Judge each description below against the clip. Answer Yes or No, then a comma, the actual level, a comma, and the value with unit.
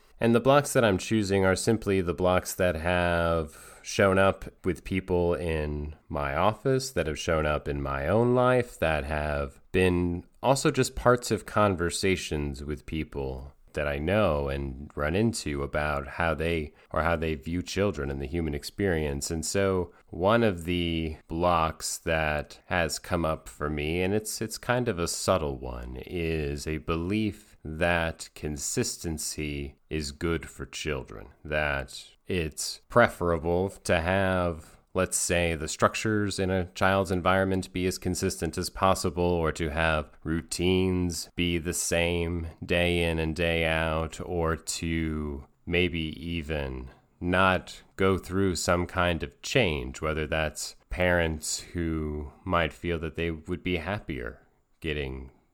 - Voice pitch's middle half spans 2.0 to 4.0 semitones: Yes, average, 3.4 semitones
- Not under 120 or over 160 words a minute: Yes, average, 150 wpm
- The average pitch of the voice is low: Yes, very low, 85 Hz